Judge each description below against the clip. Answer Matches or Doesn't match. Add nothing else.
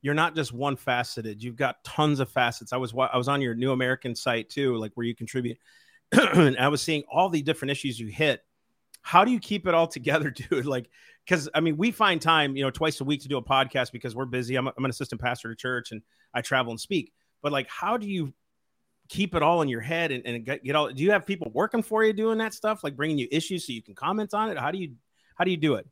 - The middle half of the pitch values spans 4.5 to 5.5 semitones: Matches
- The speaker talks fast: Matches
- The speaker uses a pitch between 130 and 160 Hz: Matches